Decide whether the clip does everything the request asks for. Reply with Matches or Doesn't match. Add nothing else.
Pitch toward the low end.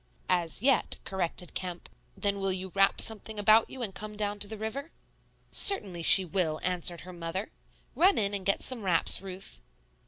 Doesn't match